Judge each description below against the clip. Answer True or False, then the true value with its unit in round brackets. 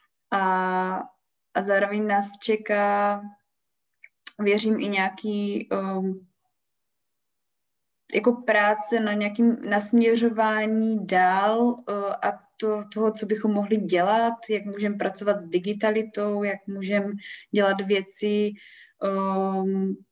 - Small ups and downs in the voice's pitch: True (1.6 semitones)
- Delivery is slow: True (100 wpm)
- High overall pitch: True (205 Hz)